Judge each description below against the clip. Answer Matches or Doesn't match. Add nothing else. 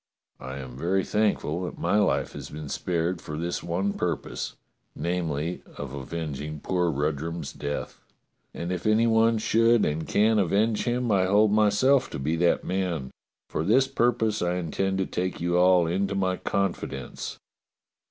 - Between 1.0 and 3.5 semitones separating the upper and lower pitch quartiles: Doesn't match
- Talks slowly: Doesn't match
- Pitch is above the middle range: Doesn't match